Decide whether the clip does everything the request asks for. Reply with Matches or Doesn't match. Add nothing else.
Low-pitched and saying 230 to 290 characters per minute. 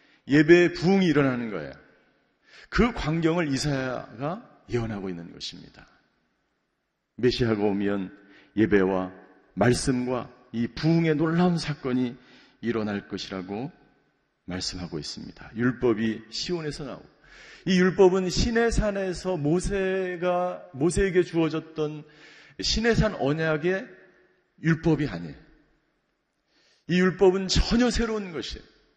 Doesn't match